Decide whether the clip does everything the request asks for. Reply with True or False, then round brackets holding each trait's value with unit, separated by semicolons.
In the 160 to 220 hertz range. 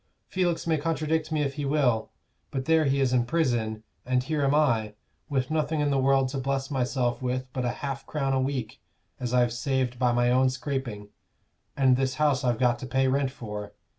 False (130 Hz)